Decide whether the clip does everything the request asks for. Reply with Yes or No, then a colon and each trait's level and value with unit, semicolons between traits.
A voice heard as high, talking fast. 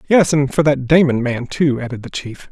No: medium, 140 Hz; fast, 240 wpm